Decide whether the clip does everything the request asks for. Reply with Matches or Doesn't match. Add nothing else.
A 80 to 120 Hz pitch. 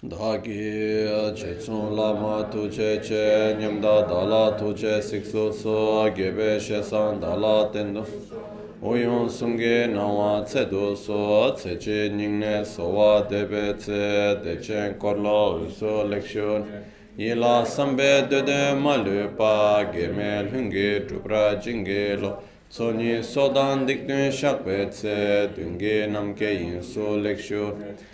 Matches